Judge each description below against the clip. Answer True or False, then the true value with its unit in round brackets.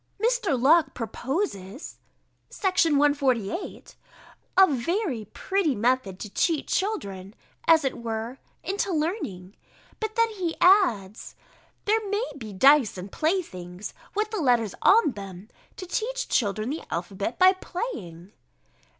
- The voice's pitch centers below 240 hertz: False (280 Hz)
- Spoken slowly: True (125 wpm)